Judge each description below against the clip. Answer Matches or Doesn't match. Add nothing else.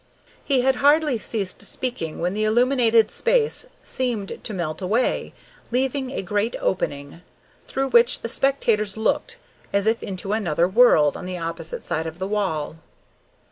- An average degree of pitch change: Doesn't match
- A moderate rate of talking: Matches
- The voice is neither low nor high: Doesn't match